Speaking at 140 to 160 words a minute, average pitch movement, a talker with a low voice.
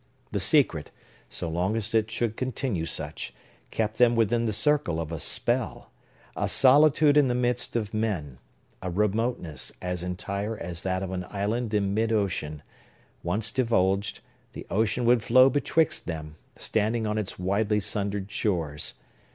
Yes: average, 155 wpm; average, 4.3 semitones; low, 105 Hz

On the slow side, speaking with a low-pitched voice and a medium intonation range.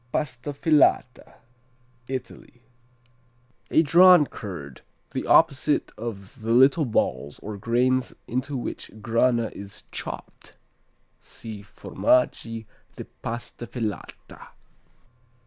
Yes: slow, 90 wpm; low, 120 Hz; average, 3.9 semitones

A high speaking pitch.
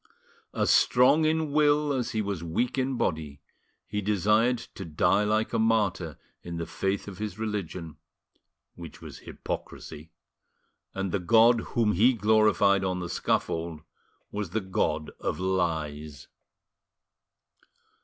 No: low, 100 Hz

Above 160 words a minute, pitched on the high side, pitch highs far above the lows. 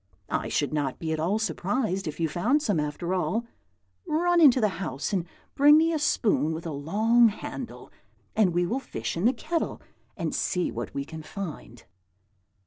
Yes: average, 185 wpm; high, 195 Hz; wide, 7.2 semitones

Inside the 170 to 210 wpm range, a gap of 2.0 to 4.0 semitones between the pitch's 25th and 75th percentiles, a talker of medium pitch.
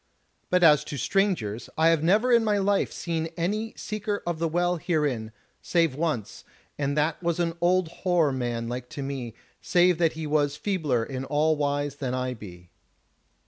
No: average, 180 wpm; average, 4.7 semitones; medium, 155 Hz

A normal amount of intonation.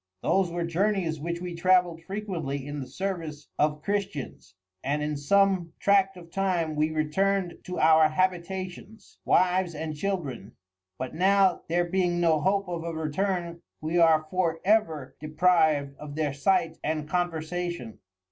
Yes: average, 3.3 semitones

